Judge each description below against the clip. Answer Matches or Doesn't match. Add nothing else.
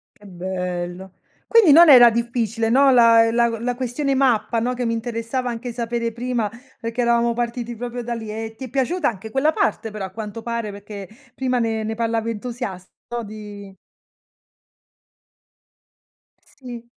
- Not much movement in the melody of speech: Matches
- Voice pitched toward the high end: Matches